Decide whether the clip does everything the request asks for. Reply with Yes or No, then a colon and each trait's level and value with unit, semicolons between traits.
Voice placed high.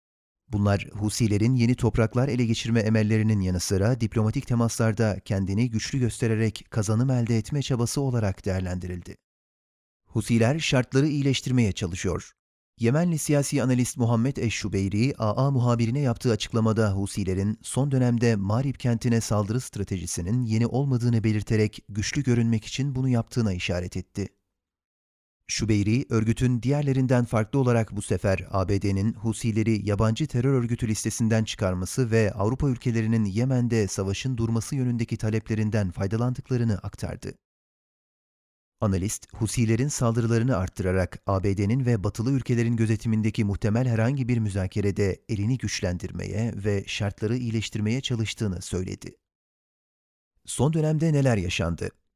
No: low, 110 Hz